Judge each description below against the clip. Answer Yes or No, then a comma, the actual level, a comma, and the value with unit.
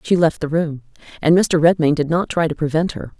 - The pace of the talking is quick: Yes, fast, 245 wpm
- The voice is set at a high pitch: No, medium, 160 Hz